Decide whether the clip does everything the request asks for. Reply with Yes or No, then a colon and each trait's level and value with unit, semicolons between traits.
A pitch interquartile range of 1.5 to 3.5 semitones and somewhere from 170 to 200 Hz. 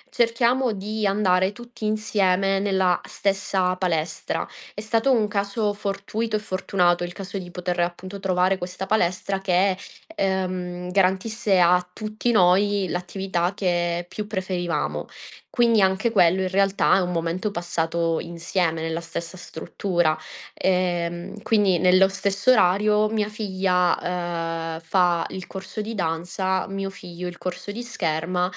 Yes: narrow, 2.5 semitones; high, 190 Hz